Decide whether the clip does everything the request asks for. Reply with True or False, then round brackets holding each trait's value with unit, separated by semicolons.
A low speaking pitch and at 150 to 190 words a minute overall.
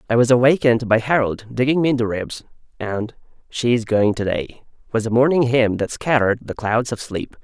False (120 Hz; 200 wpm)